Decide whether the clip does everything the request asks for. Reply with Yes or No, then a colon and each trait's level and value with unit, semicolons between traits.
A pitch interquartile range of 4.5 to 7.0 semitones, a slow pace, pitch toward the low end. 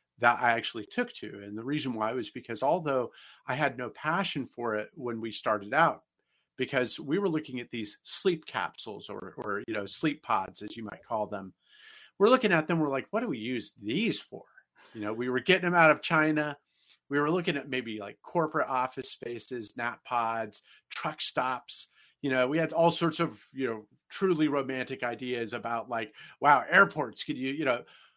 No: average, 5.2 semitones; average, 200 wpm; low, 130 Hz